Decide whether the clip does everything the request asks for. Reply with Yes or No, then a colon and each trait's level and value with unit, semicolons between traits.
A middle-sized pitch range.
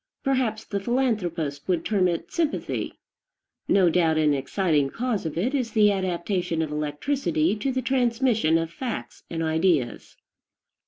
No: wide, 6.5 semitones